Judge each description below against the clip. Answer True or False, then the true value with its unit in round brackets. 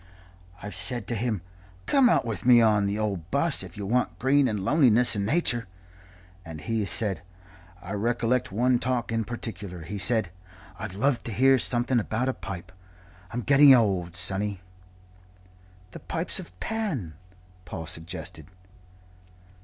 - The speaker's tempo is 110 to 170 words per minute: True (155 wpm)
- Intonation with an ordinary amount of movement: True (5.0 semitones)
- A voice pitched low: True (110 Hz)